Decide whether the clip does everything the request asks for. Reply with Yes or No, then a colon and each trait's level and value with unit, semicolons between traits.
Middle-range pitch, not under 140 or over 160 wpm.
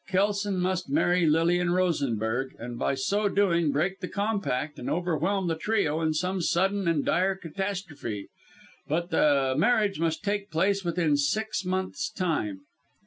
Yes: medium, 175 Hz; average, 145 wpm